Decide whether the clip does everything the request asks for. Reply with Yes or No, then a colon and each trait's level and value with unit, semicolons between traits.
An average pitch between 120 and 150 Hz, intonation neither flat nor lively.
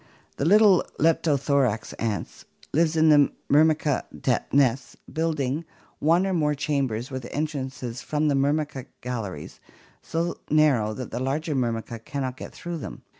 Yes: medium, 140 Hz; average, 3.6 semitones